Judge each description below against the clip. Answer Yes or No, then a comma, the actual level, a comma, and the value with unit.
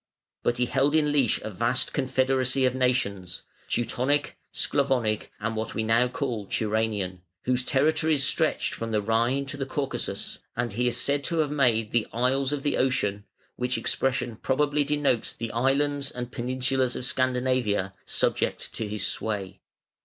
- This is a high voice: No, low, 125 Hz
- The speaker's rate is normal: Yes, average, 160 wpm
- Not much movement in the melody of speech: No, average, 3.3 semitones